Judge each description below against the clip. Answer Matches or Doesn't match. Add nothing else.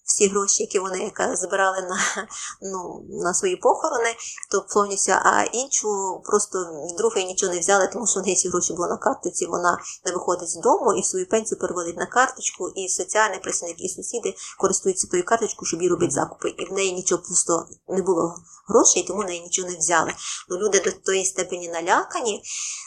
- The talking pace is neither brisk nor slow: Doesn't match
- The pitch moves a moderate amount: Matches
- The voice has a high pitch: Matches